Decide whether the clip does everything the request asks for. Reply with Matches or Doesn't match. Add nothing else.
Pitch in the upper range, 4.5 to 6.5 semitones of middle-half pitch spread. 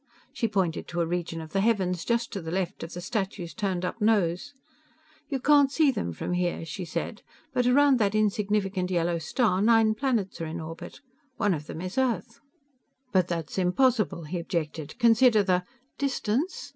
Matches